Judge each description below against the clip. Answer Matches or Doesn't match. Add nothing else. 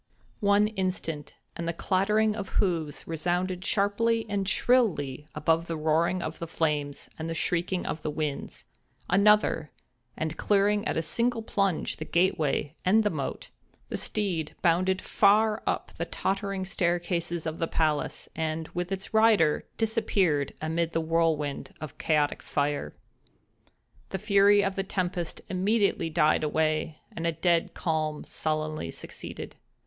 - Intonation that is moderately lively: Matches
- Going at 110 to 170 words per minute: Matches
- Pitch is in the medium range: Matches